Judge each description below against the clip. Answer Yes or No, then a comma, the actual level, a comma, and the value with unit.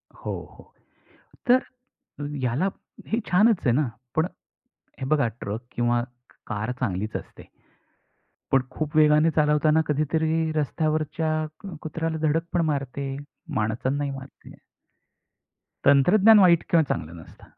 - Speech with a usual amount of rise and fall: Yes, average, 3.5 semitones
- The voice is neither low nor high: Yes, medium, 150 Hz